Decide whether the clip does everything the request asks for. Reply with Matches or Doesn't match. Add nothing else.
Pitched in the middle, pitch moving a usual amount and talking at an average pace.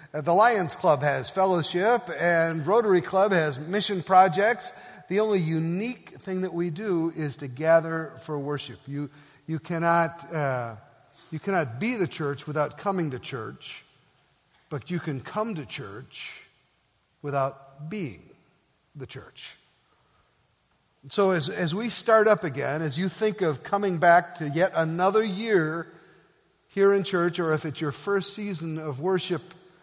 Matches